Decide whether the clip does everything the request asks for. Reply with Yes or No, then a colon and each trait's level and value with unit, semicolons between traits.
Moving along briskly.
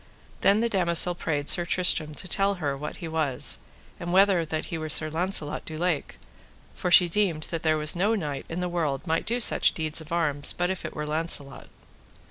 Yes: fast, 210 wpm